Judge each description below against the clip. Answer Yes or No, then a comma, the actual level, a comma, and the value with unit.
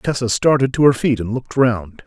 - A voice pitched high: No, low, 120 Hz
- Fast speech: Yes, fast, 235 wpm